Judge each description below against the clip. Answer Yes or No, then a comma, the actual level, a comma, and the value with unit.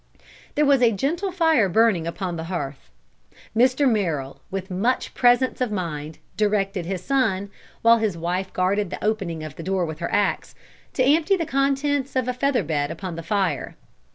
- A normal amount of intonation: No, wide, 6.9 semitones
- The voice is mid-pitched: No, high, 205 Hz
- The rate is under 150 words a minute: No, average, 180 wpm